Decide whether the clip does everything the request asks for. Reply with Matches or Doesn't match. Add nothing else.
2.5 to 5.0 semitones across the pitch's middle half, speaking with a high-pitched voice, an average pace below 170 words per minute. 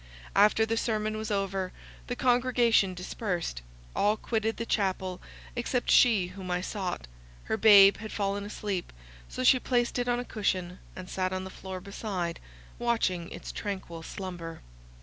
Matches